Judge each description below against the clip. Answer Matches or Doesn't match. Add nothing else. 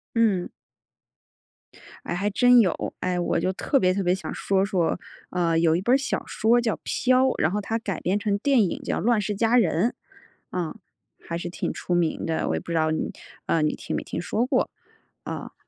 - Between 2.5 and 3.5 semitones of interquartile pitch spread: Doesn't match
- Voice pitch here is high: Matches